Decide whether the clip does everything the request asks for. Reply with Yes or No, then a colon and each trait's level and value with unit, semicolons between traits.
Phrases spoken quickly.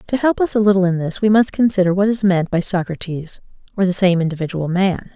Yes: fast, 235 wpm